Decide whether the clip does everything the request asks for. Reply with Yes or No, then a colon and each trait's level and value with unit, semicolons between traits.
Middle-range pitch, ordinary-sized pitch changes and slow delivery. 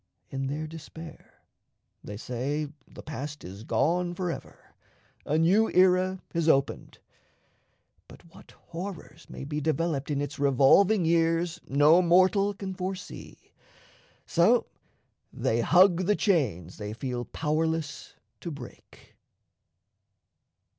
Yes: medium, 160 Hz; average, 4.3 semitones; slow, 115 wpm